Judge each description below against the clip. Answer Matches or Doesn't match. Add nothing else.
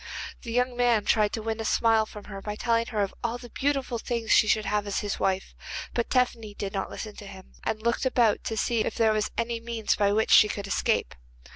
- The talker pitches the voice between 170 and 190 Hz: Doesn't match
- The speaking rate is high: Matches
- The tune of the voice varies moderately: Doesn't match